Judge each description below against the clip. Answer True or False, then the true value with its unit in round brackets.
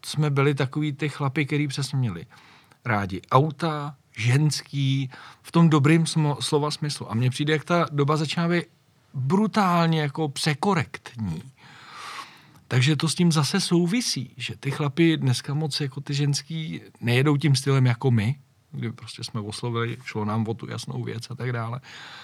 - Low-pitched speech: False (145 Hz)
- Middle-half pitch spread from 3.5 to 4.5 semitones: True (3.9 semitones)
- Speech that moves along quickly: False (160 wpm)